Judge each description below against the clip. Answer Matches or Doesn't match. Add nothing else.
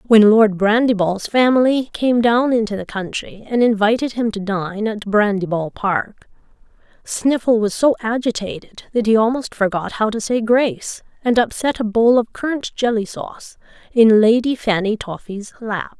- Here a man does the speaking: Doesn't match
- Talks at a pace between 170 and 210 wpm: Doesn't match